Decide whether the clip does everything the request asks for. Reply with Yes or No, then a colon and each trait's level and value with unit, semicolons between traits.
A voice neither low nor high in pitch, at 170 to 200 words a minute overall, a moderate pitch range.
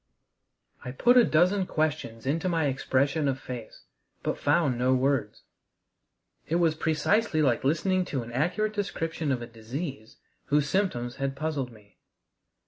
No: medium, 145 Hz; average, 145 wpm; average, 4.6 semitones